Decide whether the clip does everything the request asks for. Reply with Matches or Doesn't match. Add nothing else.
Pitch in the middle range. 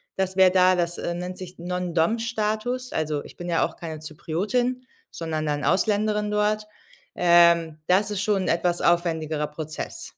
Matches